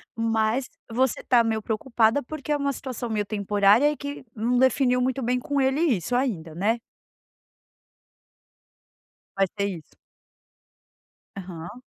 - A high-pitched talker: Yes, high, 235 Hz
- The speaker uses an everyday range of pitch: Yes, average, 4.0 semitones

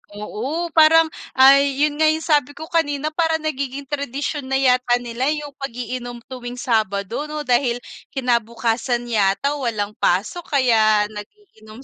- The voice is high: Yes, very high, 260 Hz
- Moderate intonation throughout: Yes, average, 4.0 semitones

